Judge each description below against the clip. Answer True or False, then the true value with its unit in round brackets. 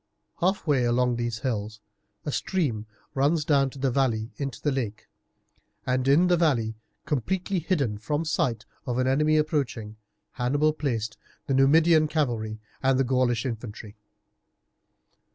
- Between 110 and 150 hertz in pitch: True (135 Hz)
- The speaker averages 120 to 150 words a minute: True (140 wpm)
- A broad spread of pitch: False (4.6 semitones)